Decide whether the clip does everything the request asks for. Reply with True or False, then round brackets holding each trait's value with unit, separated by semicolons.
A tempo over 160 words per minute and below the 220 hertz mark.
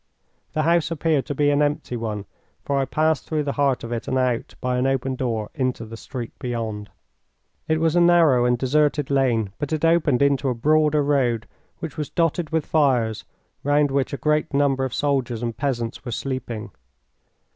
True (190 wpm; 135 Hz)